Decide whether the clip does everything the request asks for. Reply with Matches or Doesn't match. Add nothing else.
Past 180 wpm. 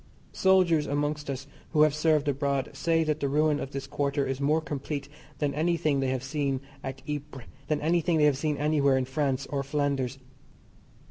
Matches